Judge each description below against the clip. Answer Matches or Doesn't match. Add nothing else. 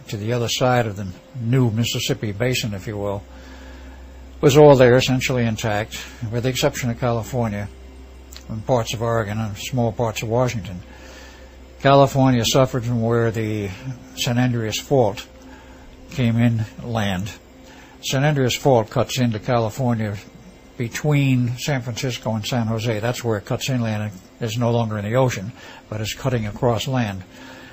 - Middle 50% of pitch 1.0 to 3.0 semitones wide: Doesn't match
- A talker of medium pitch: Doesn't match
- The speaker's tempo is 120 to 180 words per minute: Matches